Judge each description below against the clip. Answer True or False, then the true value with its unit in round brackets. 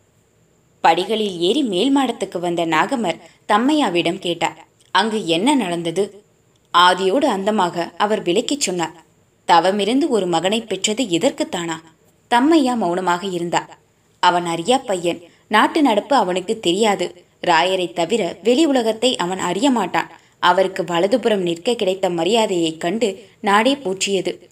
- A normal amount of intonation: True (4.9 semitones)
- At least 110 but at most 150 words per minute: True (115 wpm)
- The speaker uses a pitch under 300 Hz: True (190 Hz)